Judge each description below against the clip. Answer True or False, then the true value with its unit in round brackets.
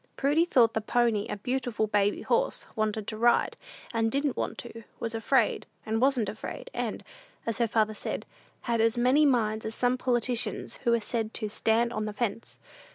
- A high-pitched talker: True (230 Hz)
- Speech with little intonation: True (2.3 semitones)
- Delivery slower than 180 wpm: False (185 wpm)